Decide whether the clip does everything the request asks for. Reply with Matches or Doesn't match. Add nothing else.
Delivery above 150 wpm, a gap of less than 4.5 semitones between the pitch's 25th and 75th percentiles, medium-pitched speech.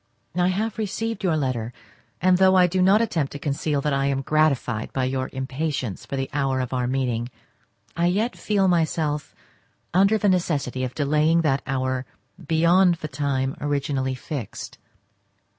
Doesn't match